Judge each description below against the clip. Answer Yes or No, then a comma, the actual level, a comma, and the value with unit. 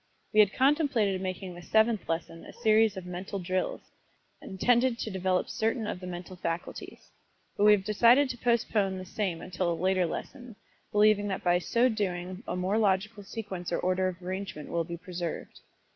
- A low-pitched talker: No, high, 190 Hz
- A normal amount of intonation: Yes, average, 3.2 semitones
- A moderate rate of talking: Yes, average, 180 wpm